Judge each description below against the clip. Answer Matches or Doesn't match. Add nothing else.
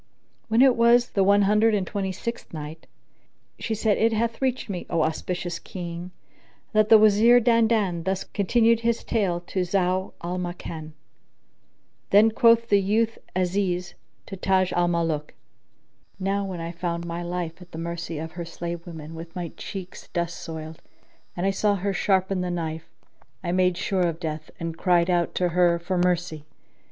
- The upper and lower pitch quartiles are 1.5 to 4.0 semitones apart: Matches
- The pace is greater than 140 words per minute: Matches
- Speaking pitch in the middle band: Matches